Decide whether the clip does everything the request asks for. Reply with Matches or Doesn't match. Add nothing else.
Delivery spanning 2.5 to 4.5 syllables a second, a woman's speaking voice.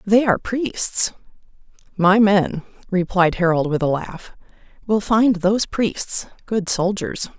Matches